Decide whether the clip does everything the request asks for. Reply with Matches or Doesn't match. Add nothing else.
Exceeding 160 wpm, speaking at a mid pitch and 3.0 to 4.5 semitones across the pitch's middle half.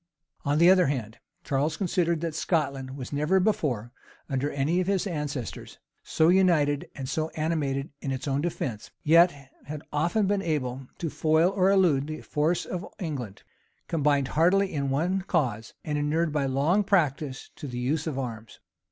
Matches